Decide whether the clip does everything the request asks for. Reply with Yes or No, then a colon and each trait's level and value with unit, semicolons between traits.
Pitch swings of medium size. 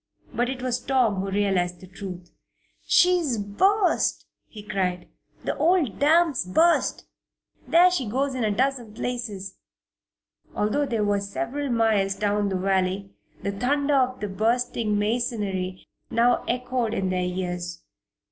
Yes: average, 4.8 semitones